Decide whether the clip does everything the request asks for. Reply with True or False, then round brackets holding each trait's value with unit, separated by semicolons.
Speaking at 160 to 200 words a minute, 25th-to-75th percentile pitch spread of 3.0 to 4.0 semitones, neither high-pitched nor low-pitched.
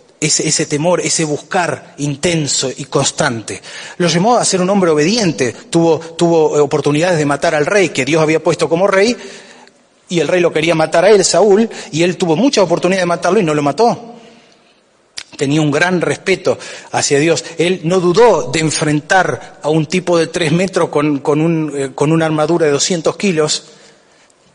True (185 wpm; 3.4 semitones; 165 Hz)